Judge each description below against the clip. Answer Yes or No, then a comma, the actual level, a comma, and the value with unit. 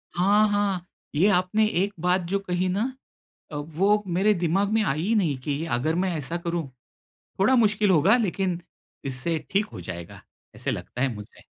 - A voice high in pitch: No, medium, 180 Hz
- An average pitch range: Yes, average, 4.3 semitones